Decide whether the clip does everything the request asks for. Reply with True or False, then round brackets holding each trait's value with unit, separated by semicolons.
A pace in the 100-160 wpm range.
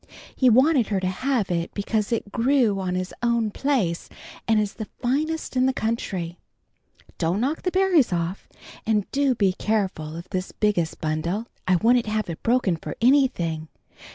False (170 wpm)